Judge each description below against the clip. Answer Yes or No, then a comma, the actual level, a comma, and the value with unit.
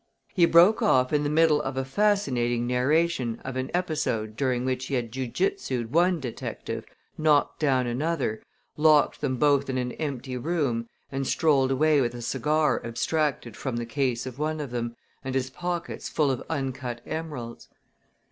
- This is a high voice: No, low, 135 Hz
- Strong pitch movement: No, average, 3.9 semitones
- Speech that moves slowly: No, average, 170 wpm